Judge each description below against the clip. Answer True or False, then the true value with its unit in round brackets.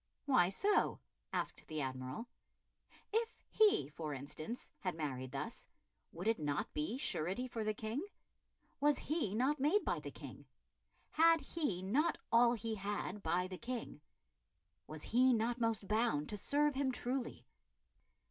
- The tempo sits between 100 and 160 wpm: True (145 wpm)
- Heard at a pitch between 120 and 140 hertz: False (225 Hz)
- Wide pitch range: True (7.5 semitones)